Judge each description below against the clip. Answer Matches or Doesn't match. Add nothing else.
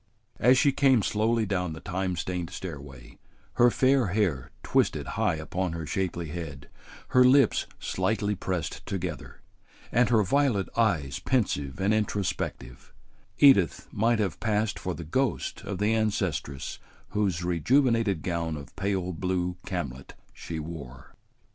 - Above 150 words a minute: Doesn't match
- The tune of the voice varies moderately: Matches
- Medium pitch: Doesn't match